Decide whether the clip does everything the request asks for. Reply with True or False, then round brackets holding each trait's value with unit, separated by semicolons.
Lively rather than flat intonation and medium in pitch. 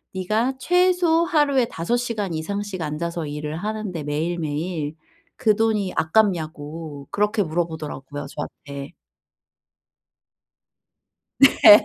True (6.0 semitones; 175 Hz)